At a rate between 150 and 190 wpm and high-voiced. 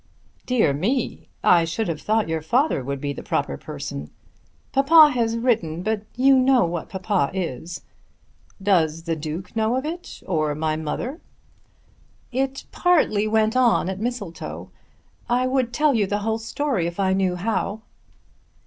Yes: average, 155 wpm; high, 210 Hz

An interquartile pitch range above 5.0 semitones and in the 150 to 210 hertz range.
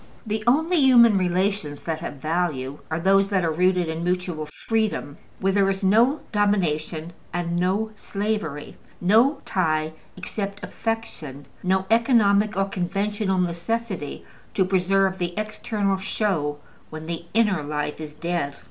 No: average, 4.2 semitones; high, 190 Hz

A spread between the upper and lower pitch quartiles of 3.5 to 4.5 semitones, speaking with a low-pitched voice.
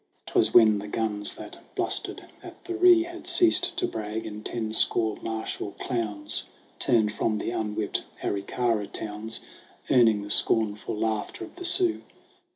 No: average, 3.0 semitones; low, 110 Hz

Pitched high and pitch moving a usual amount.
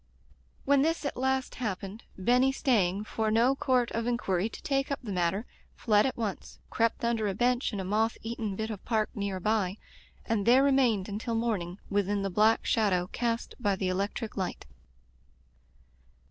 Yes: high, 220 Hz; average, 3.6 semitones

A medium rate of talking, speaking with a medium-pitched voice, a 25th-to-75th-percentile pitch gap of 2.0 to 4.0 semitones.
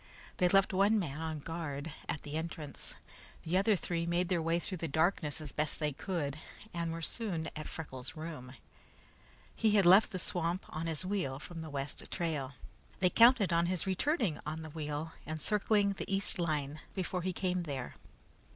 Yes: average, 185 wpm; medium, 165 Hz; average, 3.4 semitones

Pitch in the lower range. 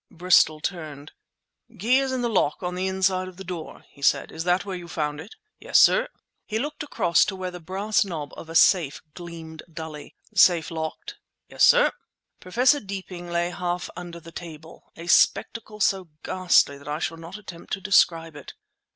No: medium, 175 Hz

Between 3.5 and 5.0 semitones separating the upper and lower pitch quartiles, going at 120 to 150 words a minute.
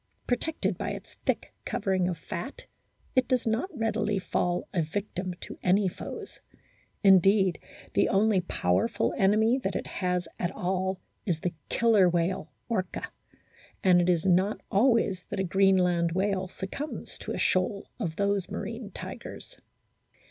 No: average, 2.9 semitones; average, 145 wpm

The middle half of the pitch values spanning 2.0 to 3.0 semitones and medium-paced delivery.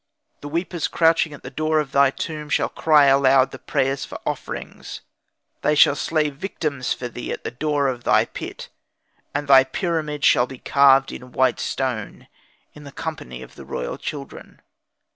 Yes: narrow, 2.6 semitones; average, 175 wpm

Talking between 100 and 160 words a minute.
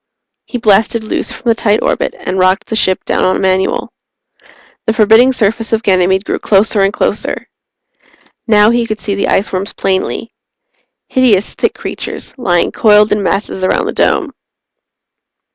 Yes: average, 155 wpm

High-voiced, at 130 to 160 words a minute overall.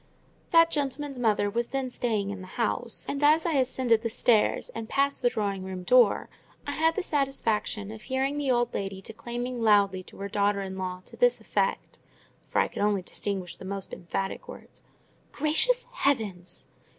No: high, 230 Hz; average, 180 wpm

